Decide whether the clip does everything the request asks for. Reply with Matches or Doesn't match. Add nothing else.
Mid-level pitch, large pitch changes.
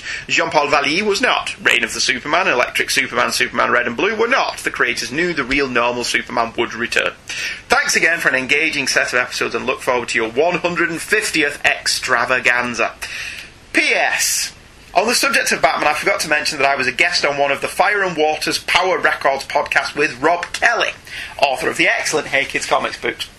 Doesn't match